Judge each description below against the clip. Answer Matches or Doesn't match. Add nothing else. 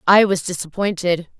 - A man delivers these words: Doesn't match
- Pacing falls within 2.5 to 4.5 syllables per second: Doesn't match